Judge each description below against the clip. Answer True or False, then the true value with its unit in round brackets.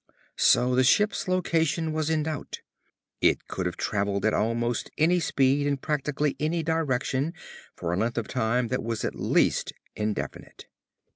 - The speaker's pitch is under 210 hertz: True (135 Hz)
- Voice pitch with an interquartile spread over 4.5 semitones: True (5.3 semitones)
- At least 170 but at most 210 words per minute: False (155 wpm)